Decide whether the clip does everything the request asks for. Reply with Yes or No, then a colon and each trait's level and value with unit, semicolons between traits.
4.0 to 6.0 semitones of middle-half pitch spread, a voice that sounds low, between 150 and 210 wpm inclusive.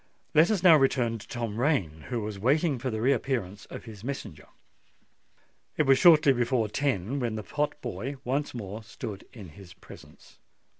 Yes: average, 4.9 semitones; low, 120 Hz; average, 170 wpm